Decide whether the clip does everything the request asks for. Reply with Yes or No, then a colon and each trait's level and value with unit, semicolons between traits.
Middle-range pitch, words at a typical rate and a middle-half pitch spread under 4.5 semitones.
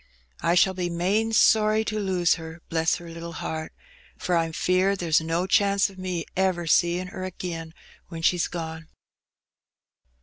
Yes: medium, 175 Hz; average, 160 wpm; narrow, 2.4 semitones